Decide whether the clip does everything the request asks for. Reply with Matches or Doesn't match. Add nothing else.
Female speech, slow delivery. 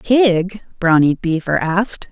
Matches